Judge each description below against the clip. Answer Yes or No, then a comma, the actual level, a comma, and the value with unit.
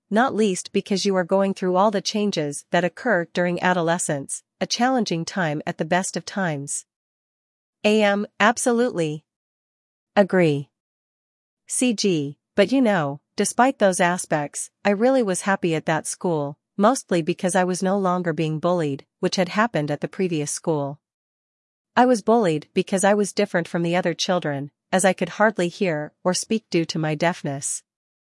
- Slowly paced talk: No, average, 160 wpm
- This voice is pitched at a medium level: Yes, medium, 180 Hz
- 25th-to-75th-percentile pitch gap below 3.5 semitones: No, average, 4.1 semitones